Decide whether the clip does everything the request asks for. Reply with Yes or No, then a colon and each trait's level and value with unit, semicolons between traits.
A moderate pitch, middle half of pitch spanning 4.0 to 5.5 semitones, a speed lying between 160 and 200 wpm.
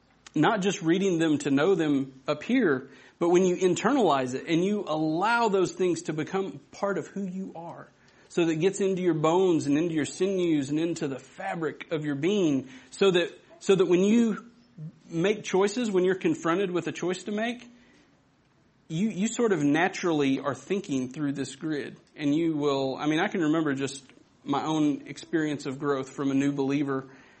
Yes: medium, 165 Hz; average, 5.0 semitones; average, 195 wpm